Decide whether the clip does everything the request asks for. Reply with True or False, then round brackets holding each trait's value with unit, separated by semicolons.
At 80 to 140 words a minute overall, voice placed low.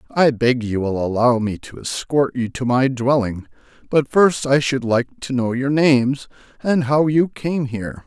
False (195 wpm; 130 Hz)